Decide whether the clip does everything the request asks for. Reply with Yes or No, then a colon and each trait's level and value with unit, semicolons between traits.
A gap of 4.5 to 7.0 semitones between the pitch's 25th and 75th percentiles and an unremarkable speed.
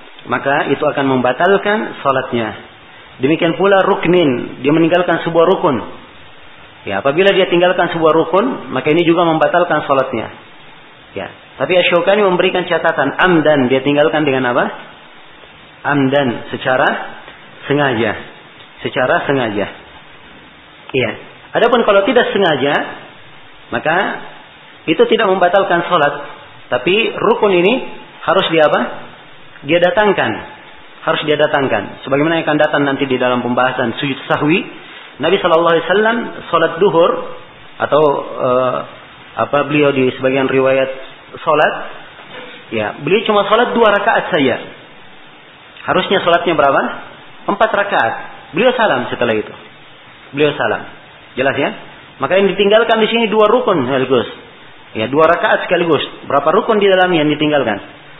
Yes: average, 5.3 semitones; average, 125 wpm